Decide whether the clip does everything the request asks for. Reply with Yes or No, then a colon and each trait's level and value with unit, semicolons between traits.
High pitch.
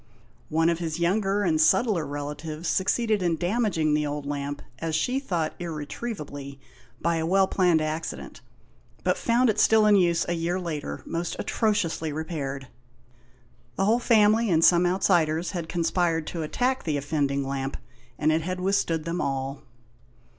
No: medium, 165 Hz